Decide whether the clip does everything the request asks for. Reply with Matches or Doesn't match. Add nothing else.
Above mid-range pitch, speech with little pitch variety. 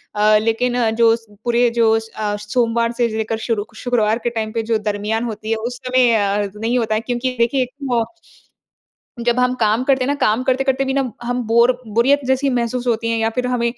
Matches